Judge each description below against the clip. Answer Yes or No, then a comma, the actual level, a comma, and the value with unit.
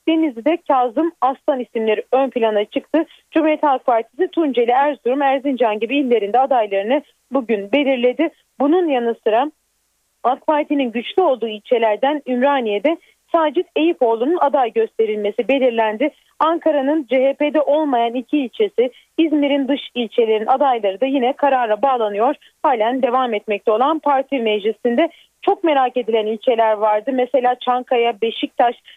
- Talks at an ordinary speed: Yes, average, 120 wpm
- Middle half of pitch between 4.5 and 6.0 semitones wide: No, average, 4.0 semitones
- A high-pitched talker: Yes, very high, 265 Hz